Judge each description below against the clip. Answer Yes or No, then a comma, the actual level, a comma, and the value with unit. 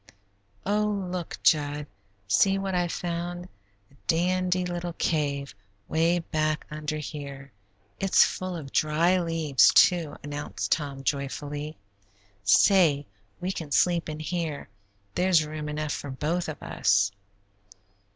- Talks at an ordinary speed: No, slow, 120 wpm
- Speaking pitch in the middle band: Yes, medium, 160 Hz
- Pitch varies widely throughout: No, average, 3.3 semitones